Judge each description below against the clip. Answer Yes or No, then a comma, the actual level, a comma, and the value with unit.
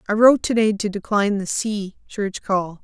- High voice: Yes, high, 205 Hz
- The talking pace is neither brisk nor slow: Yes, average, 190 wpm